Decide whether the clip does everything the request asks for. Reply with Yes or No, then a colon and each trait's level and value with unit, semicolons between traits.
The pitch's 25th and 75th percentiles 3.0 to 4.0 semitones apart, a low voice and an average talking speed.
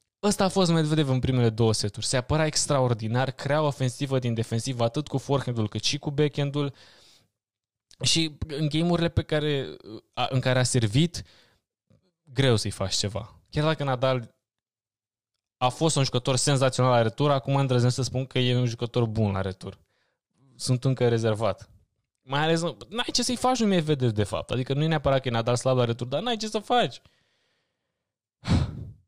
No: average, 4.4 semitones; low, 130 Hz; average, 180 wpm